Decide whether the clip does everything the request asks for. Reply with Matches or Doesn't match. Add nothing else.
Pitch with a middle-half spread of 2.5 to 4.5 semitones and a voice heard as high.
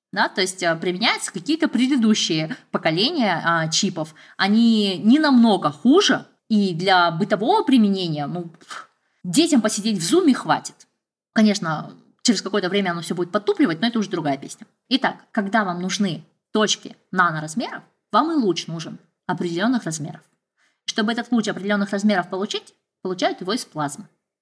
Doesn't match